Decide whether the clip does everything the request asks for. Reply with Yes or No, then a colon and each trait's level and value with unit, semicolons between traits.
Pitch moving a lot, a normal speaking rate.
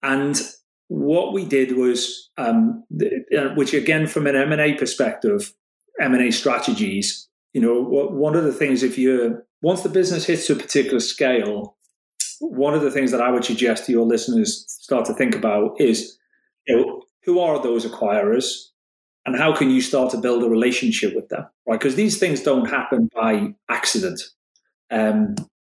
Yes: wide, 9.0 semitones; average, 165 wpm